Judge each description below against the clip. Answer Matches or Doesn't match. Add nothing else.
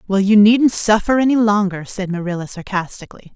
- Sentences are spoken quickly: Doesn't match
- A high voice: Matches